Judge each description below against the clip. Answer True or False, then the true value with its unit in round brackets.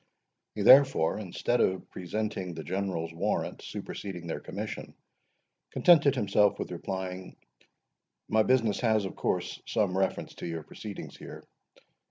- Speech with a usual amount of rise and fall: True (3.2 semitones)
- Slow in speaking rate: True (125 wpm)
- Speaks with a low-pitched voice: True (95 Hz)